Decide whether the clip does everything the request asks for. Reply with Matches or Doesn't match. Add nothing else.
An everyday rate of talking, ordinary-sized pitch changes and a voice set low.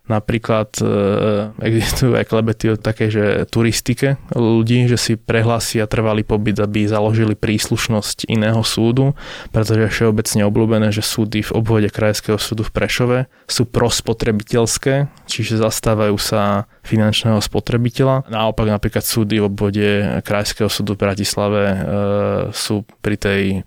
Doesn't match